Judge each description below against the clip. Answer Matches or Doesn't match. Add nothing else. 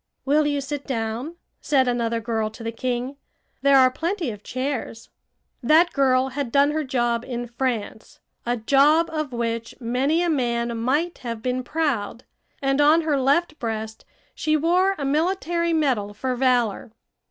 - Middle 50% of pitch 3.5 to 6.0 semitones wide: Matches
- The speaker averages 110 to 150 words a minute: Doesn't match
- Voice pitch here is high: Matches